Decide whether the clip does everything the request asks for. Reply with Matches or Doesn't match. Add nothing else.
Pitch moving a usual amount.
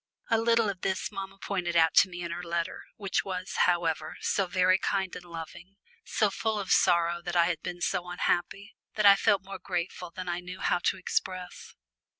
Doesn't match